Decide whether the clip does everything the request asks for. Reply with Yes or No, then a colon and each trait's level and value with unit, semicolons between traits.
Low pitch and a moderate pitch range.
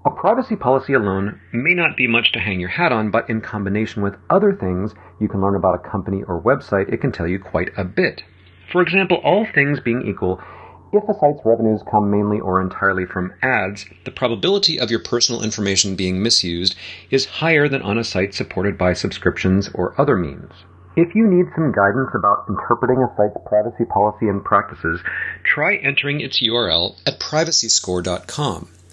No: low, 110 Hz; wide, 6.0 semitones